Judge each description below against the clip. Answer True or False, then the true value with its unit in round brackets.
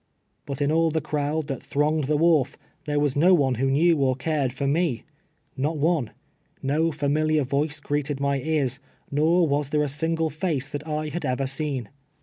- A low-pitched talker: False (150 Hz)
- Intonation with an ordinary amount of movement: False (2.2 semitones)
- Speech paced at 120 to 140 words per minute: False (185 wpm)